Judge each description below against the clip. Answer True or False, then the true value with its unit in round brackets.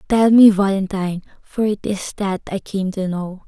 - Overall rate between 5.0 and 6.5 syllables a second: False (4.7 syllables/s)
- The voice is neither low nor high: False (195 Hz)